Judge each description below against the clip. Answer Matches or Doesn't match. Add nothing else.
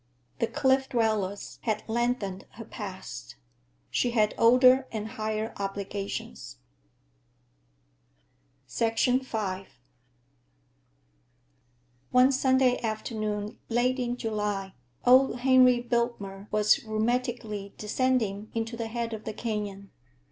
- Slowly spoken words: Matches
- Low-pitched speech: Doesn't match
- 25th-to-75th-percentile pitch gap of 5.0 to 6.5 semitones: Doesn't match